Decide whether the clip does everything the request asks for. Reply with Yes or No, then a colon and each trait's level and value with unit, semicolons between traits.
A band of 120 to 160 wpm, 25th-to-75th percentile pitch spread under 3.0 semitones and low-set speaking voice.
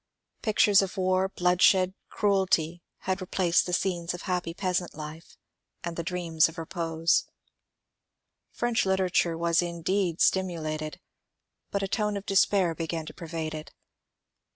No: slow, 135 wpm; narrow, 2.5 semitones; medium, 175 Hz